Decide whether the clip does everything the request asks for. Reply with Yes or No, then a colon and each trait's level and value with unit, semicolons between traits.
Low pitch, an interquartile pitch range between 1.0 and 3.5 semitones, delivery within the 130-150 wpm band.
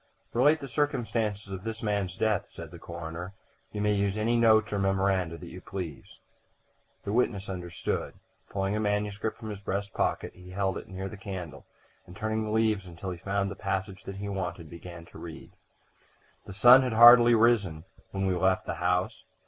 No: low, 100 Hz; average, 2.9 semitones; average, 190 wpm